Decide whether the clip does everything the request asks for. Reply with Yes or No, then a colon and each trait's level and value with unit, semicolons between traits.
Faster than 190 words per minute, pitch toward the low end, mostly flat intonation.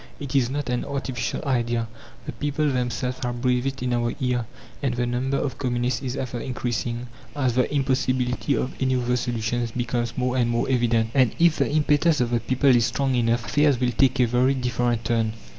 Yes: average, 200 wpm; low, 125 Hz; narrow, 1.8 semitones